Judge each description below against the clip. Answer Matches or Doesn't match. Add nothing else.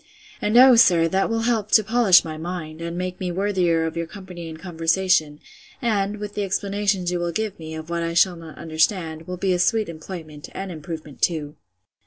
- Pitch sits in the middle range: Matches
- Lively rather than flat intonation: Doesn't match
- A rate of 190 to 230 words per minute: Matches